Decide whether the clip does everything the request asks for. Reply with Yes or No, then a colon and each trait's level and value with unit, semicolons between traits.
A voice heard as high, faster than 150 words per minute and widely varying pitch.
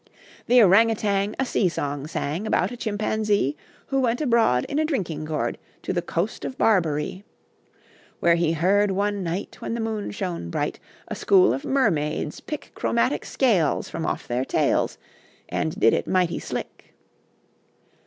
Yes: high, 195 Hz; average, 160 wpm; wide, 5.7 semitones